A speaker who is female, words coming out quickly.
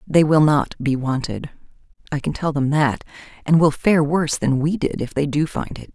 Yes: female; fast, 220 wpm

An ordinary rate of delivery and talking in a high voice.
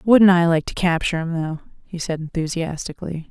No: average, 180 wpm; medium, 170 Hz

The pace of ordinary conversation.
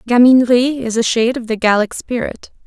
Yes: average, 180 wpm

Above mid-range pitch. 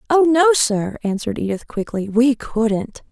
Yes: high, 240 Hz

